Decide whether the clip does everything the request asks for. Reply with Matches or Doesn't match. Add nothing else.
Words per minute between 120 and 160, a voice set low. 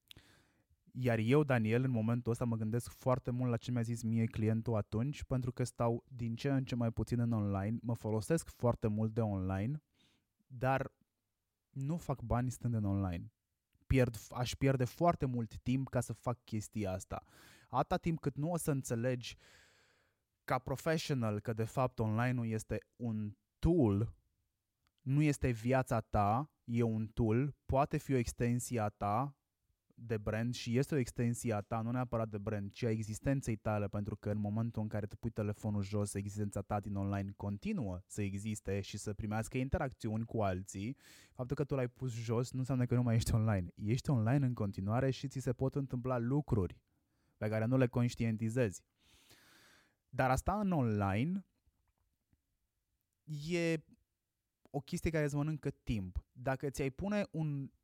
Doesn't match